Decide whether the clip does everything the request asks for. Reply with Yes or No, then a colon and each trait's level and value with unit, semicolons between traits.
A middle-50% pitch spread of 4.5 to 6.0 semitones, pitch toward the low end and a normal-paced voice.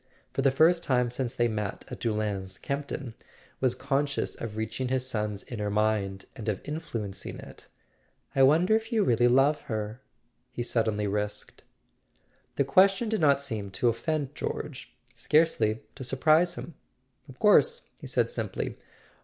Yes: wide, 5.4 semitones; low, 125 Hz; average, 160 wpm